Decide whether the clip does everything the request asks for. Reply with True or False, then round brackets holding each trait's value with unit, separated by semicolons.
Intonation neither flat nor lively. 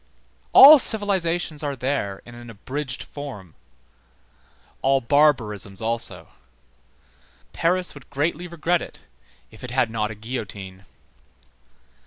False (6.4 semitones)